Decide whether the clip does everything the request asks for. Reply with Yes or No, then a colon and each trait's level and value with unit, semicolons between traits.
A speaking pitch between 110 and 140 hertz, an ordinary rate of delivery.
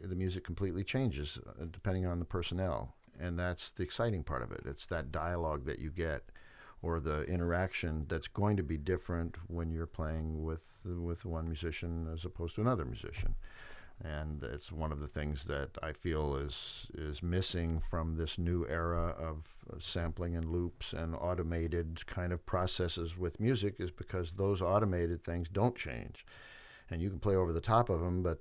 No: very low, 85 Hz; average, 180 wpm